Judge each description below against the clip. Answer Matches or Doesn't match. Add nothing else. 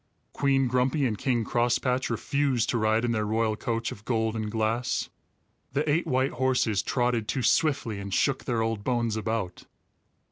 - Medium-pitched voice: Doesn't match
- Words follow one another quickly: Doesn't match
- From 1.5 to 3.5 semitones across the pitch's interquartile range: Matches